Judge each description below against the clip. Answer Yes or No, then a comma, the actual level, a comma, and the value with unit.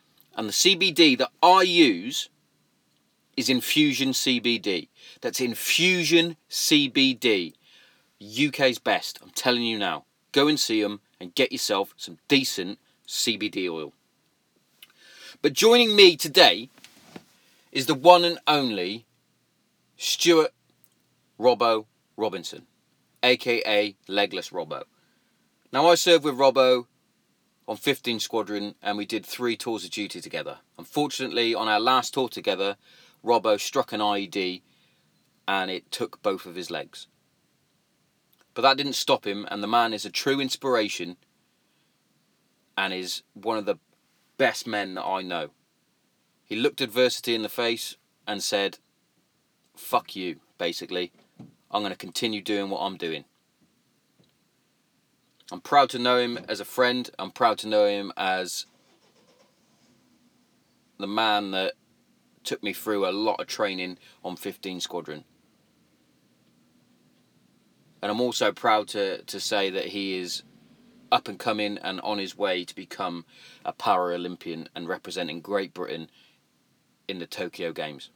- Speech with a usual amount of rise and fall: No, wide, 6.3 semitones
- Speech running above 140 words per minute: No, slow, 135 wpm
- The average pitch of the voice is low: Yes, low, 120 Hz